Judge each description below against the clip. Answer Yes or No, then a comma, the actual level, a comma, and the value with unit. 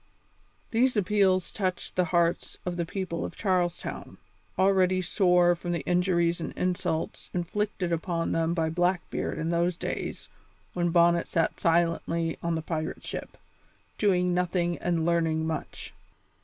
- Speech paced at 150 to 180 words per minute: No, average, 140 wpm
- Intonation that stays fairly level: Yes, narrow, 1.5 semitones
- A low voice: No, medium, 175 Hz